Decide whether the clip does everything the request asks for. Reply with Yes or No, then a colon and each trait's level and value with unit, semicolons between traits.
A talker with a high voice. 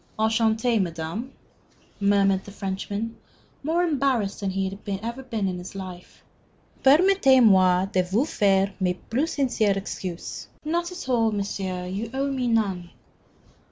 Yes: high, 205 Hz